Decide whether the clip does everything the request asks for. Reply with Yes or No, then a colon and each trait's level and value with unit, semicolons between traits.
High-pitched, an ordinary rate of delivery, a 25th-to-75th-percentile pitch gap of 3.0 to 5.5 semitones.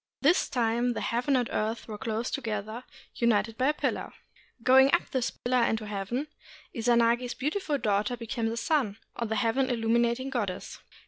No: high, 235 Hz; average, 170 wpm; narrow, 2.4 semitones